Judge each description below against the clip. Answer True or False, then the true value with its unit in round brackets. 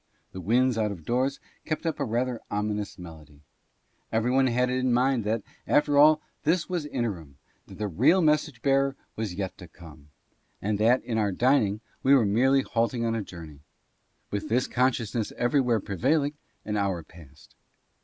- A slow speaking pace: False (175 wpm)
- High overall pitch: False (115 Hz)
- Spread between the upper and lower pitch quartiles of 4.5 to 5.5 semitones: True (5.0 semitones)